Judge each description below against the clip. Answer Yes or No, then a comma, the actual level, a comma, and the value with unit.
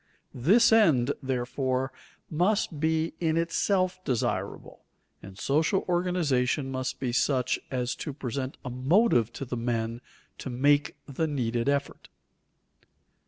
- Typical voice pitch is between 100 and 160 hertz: Yes, low, 135 Hz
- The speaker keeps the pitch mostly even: No, average, 4.6 semitones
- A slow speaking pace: Yes, slow, 120 wpm